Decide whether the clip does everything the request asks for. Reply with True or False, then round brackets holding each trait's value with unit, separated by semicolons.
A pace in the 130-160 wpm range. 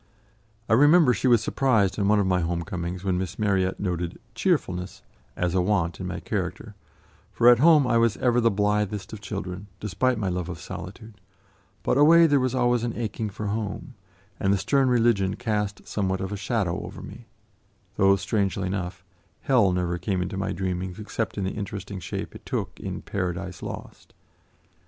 False (185 wpm)